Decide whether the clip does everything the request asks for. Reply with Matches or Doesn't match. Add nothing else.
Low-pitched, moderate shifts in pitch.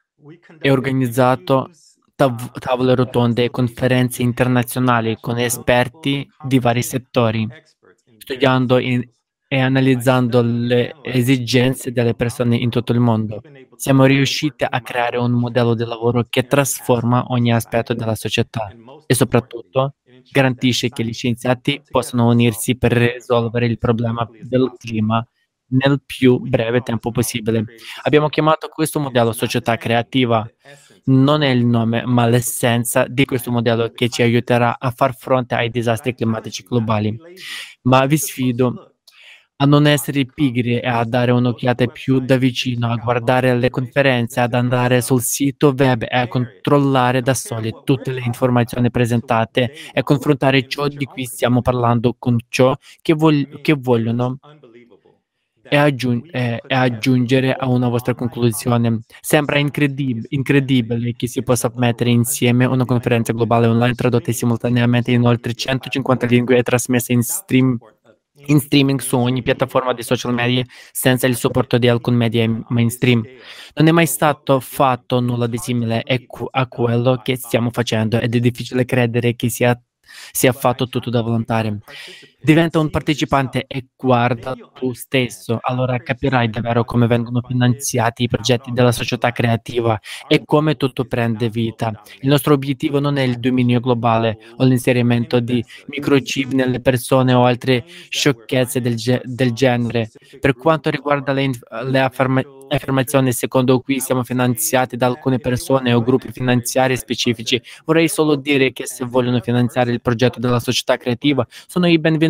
Doesn't match